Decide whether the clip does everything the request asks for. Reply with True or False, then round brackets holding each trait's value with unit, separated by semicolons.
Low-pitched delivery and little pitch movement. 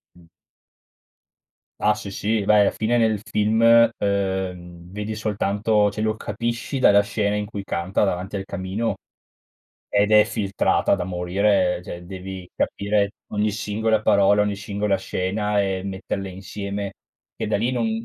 True (100 Hz; 1.8 semitones)